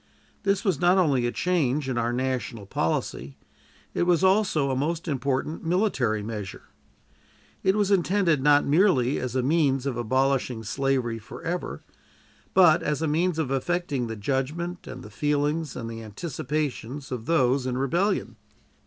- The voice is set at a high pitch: No, medium, 140 Hz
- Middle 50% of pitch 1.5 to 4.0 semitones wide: No, average, 5.2 semitones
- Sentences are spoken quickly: No, average, 155 wpm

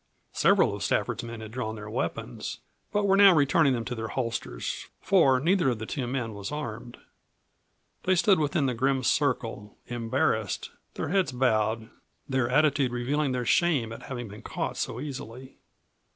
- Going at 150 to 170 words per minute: Yes, average, 165 wpm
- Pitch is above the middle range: No, low, 125 Hz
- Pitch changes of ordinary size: Yes, average, 4.4 semitones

